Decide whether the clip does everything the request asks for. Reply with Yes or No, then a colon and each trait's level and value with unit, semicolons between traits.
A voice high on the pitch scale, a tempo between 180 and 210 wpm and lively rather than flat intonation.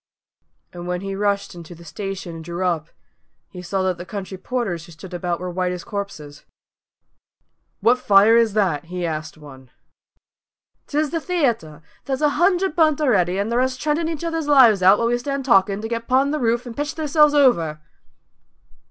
Yes: high, 200 Hz; average, 185 wpm; wide, 7.4 semitones